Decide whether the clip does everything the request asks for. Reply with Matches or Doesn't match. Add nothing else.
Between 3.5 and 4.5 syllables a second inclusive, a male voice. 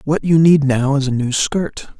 Matches